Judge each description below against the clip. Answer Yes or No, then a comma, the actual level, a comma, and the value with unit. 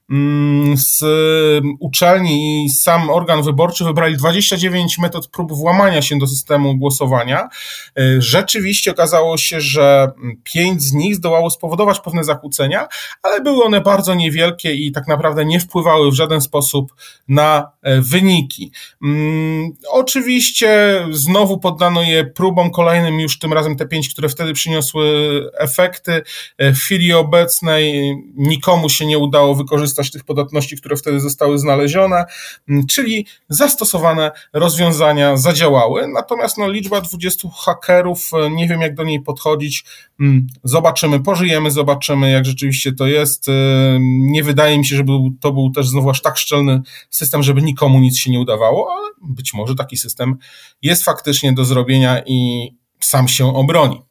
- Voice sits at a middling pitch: Yes, medium, 150 Hz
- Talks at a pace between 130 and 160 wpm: Yes, average, 140 wpm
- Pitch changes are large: No, average, 3.4 semitones